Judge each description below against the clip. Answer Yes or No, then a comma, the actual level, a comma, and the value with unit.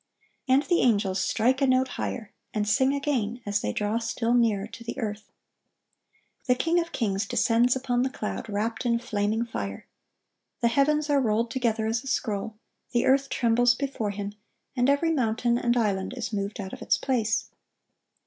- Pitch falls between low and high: No, high, 235 Hz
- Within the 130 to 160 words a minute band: No, average, 175 wpm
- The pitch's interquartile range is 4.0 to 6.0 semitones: No, average, 3.5 semitones